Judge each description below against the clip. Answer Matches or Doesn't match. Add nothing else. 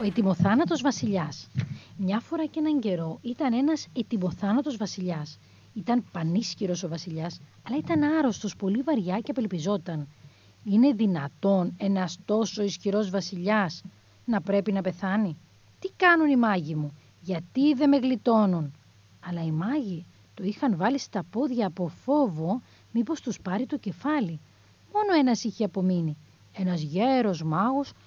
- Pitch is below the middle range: Doesn't match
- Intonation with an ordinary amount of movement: Doesn't match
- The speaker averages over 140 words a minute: Doesn't match